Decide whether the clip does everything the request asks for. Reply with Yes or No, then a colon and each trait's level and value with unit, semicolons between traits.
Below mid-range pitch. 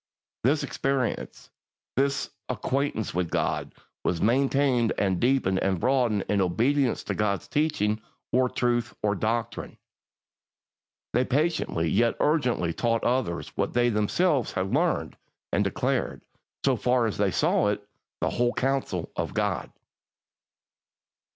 Yes: low, 120 Hz